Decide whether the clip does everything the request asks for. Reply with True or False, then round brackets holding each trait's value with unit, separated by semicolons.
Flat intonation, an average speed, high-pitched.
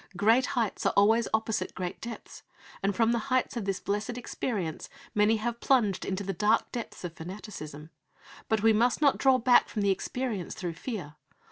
False (3.6 semitones; 180 wpm; 215 Hz)